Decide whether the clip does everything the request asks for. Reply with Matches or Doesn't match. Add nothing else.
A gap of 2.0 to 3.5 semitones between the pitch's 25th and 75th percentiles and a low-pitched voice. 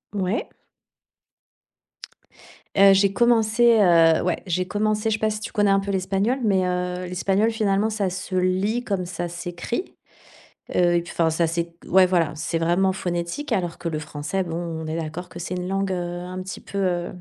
Doesn't match